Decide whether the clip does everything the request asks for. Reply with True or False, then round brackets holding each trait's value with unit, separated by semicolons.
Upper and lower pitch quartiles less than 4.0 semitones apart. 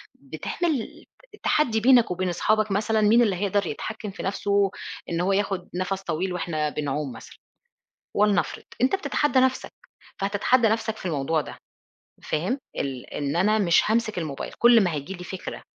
False (4.3 semitones)